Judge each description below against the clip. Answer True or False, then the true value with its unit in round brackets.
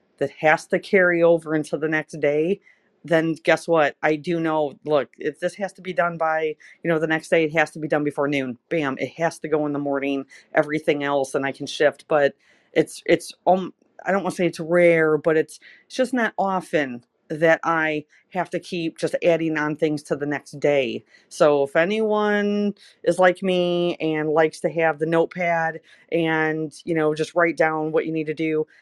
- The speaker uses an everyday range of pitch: False (2.2 semitones)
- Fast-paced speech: True (210 wpm)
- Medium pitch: True (160 Hz)